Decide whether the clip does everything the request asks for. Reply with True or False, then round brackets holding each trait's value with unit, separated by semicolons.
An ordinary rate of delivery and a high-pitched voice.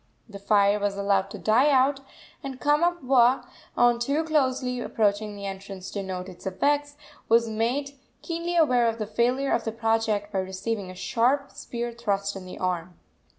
True (170 wpm; 230 Hz)